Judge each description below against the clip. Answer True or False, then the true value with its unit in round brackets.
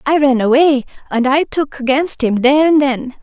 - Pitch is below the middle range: False (275 Hz)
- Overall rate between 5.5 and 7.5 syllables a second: False (5.0 syllables/s)